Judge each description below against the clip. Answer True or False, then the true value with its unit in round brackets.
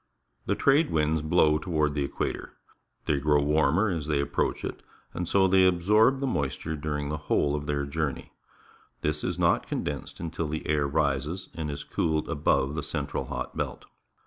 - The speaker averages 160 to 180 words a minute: True (170 wpm)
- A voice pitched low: True (75 Hz)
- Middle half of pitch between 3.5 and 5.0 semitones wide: False (2.6 semitones)